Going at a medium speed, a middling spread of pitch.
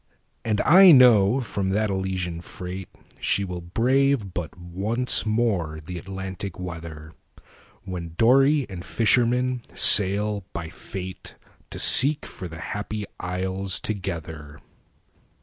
No: slow, 105 wpm; average, 4.5 semitones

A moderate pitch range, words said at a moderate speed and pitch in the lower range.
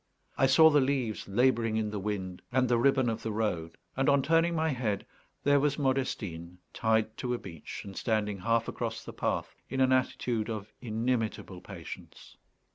Yes: average, 4.1 semitones; average, 180 wpm; low, 115 Hz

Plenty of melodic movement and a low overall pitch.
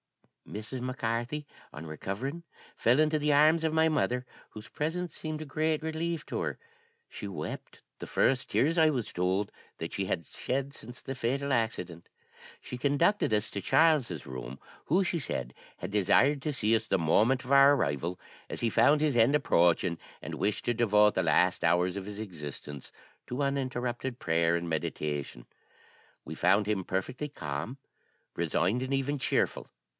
Yes: wide, 7.7 semitones; low, 120 Hz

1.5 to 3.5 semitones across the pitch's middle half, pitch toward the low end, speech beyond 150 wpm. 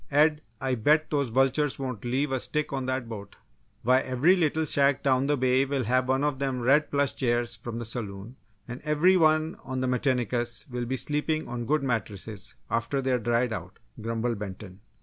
Yes: average, 3.2 semitones; low, 130 Hz; average, 190 wpm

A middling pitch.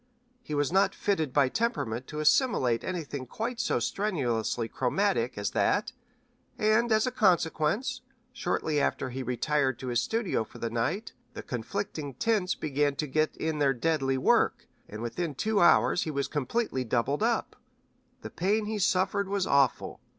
Yes: medium, 150 Hz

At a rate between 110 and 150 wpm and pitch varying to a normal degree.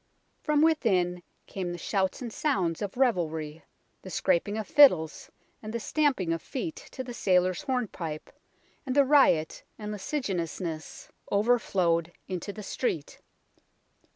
No: slow, 135 wpm; wide, 6.7 semitones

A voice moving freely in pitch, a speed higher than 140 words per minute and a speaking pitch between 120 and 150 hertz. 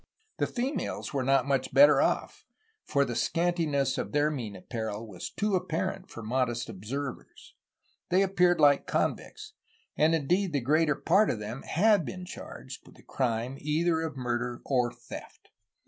Yes: wide, 5.7 semitones; average, 160 wpm; medium, 140 Hz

